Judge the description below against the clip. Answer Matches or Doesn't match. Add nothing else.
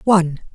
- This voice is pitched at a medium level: Matches